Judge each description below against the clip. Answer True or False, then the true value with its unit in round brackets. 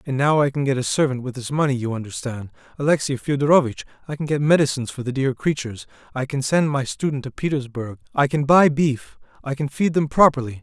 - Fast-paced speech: True (215 wpm)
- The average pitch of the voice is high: False (135 Hz)